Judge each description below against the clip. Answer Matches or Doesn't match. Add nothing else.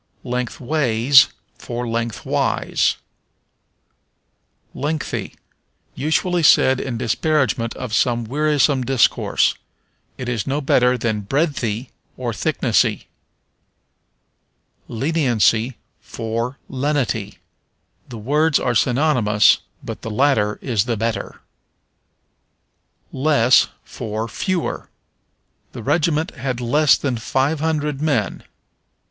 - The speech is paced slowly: Matches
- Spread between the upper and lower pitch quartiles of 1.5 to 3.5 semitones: Doesn't match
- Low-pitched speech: Matches